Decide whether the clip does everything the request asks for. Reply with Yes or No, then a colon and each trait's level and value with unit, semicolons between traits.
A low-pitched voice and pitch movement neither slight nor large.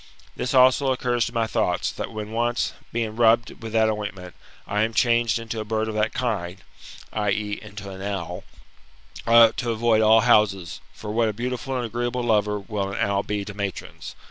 No: low, 110 Hz; narrow, 2.2 semitones